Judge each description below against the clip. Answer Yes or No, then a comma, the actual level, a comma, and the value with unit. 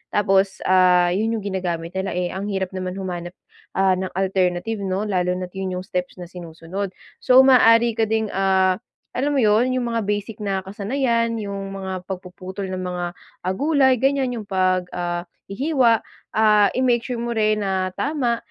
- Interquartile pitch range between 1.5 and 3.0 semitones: No, average, 3.7 semitones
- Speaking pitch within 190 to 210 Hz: Yes, high, 195 Hz